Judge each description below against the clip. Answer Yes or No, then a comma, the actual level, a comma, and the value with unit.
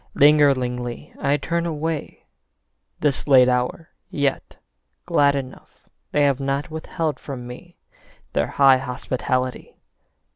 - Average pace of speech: No, slow, 110 wpm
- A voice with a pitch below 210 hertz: Yes, medium, 140 Hz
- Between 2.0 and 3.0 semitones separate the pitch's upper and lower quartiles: Yes, narrow, 2.6 semitones